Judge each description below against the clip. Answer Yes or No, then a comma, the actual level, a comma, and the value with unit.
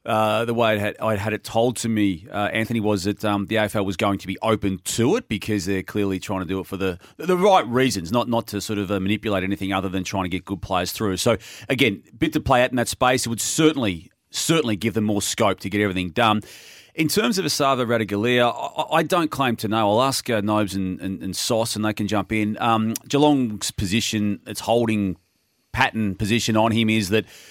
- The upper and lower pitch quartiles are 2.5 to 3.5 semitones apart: Yes, average, 2.8 semitones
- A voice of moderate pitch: No, low, 110 Hz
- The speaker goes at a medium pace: No, fast, 230 wpm